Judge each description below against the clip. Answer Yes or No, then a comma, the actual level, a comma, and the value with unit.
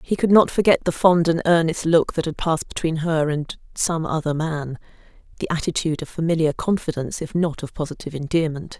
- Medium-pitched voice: Yes, medium, 160 Hz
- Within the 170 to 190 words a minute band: Yes, average, 185 wpm